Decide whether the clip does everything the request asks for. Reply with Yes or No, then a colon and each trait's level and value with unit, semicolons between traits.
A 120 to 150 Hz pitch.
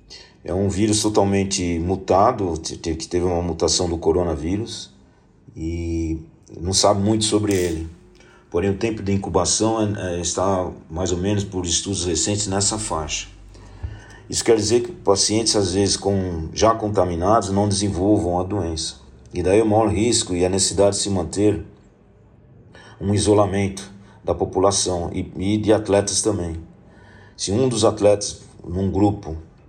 No: low, 100 Hz